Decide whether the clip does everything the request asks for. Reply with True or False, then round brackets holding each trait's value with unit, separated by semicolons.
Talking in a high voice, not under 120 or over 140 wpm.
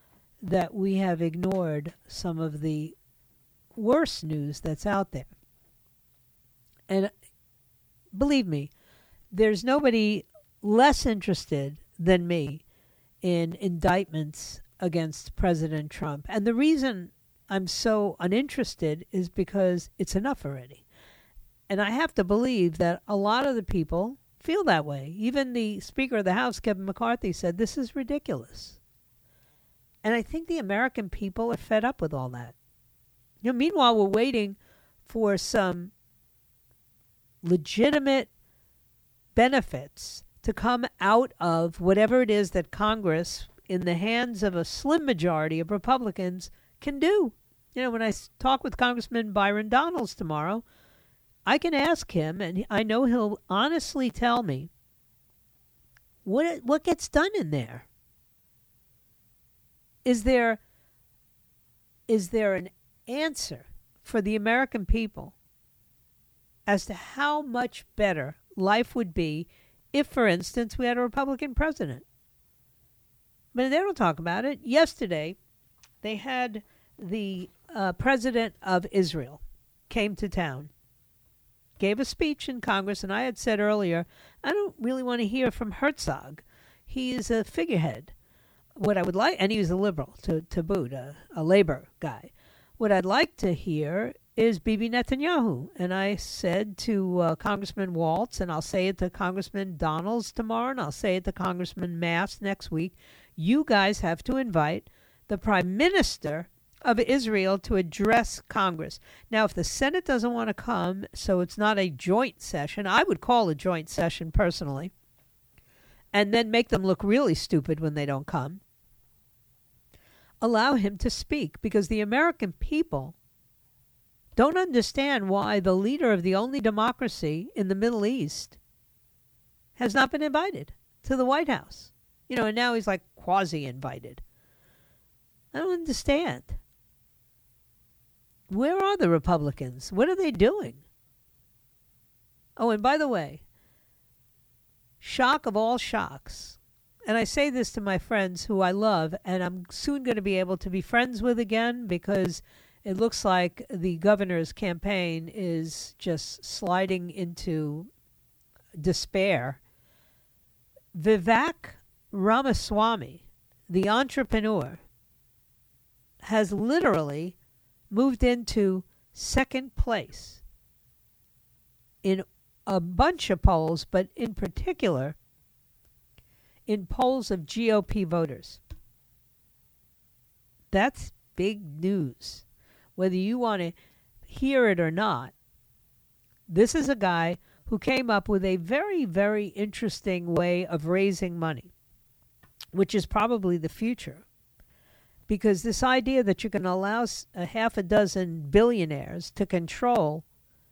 True (200 Hz; 135 wpm)